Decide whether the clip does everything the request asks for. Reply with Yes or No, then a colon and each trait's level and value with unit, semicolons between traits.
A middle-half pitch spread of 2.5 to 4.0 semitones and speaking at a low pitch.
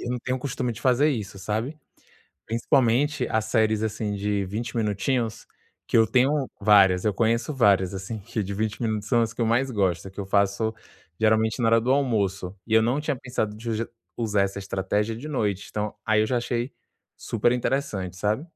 Yes: average, 2.9 semitones; low, 110 Hz